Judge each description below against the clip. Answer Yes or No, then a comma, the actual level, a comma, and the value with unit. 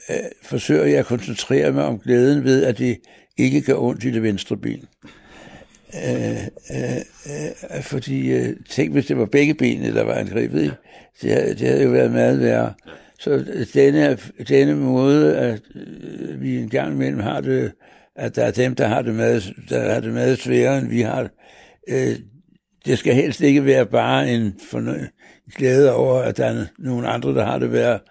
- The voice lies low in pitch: Yes, low, 125 Hz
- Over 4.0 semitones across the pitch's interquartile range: Yes, average, 4.4 semitones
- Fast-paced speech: No, average, 180 wpm